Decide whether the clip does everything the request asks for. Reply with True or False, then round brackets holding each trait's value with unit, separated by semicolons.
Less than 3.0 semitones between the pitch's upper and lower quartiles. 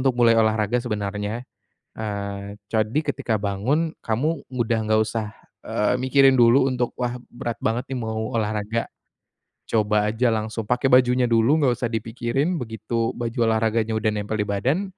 True (2.5 semitones)